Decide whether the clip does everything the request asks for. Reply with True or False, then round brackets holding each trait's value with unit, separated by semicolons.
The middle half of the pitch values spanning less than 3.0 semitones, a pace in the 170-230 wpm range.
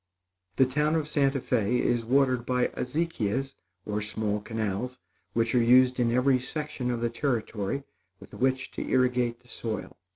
False (2.4 semitones; 160 wpm)